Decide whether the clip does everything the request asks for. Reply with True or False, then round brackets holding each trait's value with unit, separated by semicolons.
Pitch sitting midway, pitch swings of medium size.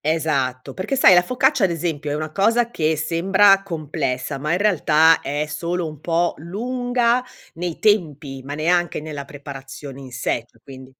True (160 Hz; 4.7 semitones)